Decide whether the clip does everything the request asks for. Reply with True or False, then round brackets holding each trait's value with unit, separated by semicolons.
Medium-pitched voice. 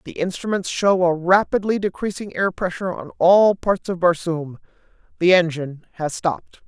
True (180 Hz)